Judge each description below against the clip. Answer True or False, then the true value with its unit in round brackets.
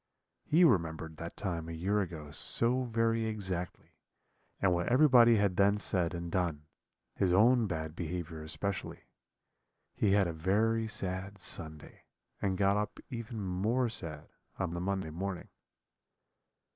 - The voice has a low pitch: True (95 Hz)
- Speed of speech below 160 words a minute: True (140 wpm)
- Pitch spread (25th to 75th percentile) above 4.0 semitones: True (4.5 semitones)